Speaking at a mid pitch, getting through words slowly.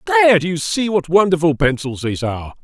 No: medium, 150 Hz; fast, 205 wpm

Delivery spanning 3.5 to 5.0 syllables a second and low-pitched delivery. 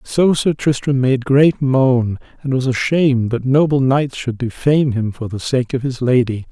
Yes: 4.6 syllables/s; low, 130 Hz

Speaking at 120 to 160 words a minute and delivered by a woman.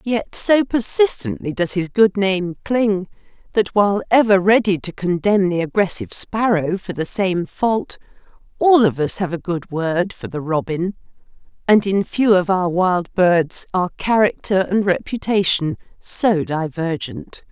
Yes: average, 150 wpm; female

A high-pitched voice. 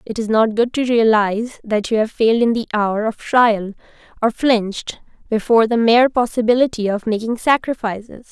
Yes: high, 225 Hz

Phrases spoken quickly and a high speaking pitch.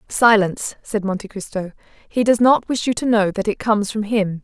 Yes: fast, 215 wpm; high, 210 Hz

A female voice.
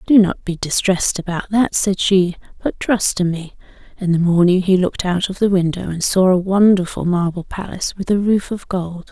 Yes: female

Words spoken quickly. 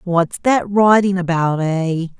No: slow, 135 wpm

